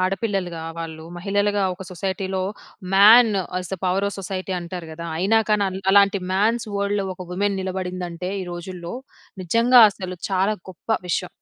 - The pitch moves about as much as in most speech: No, narrow, 2.0 semitones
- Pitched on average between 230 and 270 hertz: No, high, 190 Hz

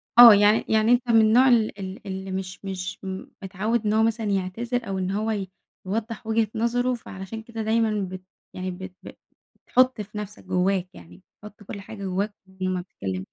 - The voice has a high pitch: Yes, high, 210 Hz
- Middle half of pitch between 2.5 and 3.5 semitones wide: Yes, average, 3.0 semitones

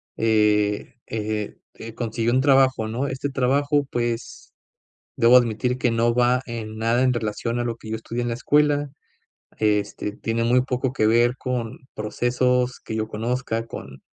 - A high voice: No, low, 120 Hz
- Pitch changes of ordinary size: No, narrow, 2.3 semitones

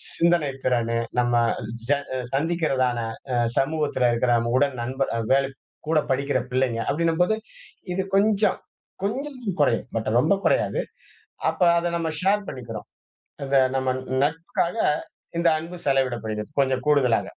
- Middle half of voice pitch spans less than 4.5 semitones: No, average, 5.0 semitones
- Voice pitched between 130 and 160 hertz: Yes, medium, 140 Hz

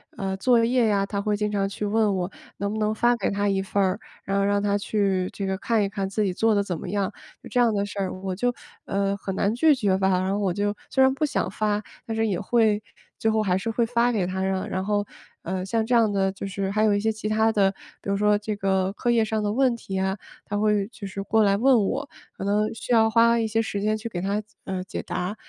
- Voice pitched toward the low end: No, high, 205 Hz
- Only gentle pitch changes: Yes, narrow, 2.2 semitones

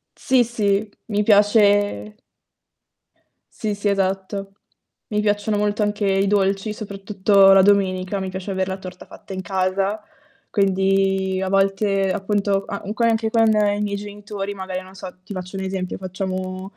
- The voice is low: No, high, 195 Hz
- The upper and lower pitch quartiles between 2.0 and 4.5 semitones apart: No, narrow, 1.5 semitones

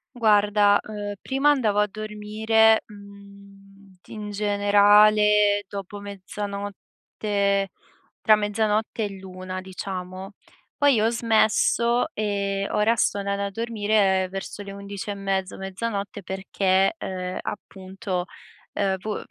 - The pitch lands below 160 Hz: No, high, 205 Hz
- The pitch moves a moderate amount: No, narrow, 1.4 semitones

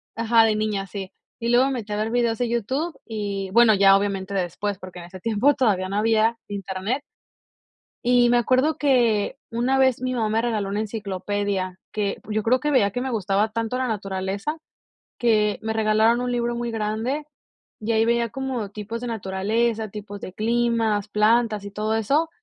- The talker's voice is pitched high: Yes, high, 220 Hz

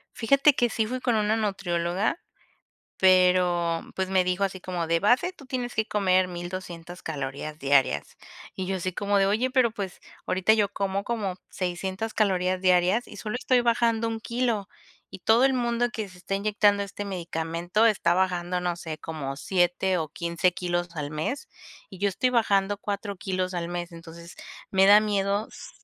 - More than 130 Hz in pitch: Yes, high, 190 Hz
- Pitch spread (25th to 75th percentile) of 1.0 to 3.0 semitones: No, average, 3.5 semitones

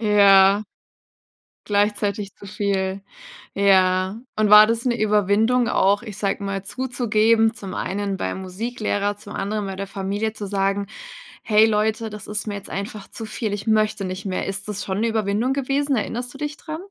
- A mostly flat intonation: Yes, narrow, 2.0 semitones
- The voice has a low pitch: No, high, 210 Hz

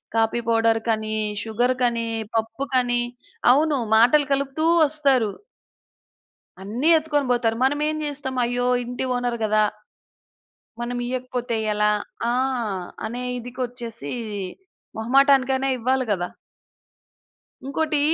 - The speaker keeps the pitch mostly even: No, average, 3.0 semitones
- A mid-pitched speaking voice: No, high, 245 Hz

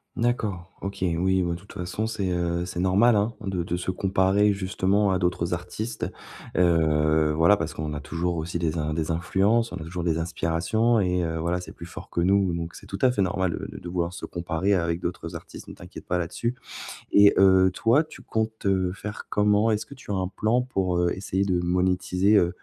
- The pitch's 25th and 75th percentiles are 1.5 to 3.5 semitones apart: Yes, average, 2.9 semitones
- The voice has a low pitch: Yes, very low, 90 Hz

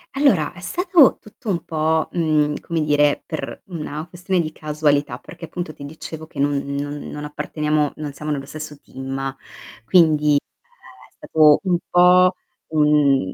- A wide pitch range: No, narrow, 2.5 semitones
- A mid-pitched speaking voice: Yes, medium, 155 Hz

